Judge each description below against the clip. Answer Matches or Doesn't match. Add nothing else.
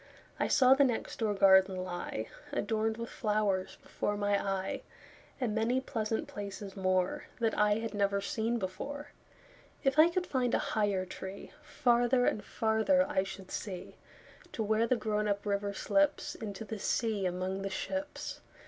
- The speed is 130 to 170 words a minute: Matches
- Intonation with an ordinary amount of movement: Matches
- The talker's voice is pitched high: Matches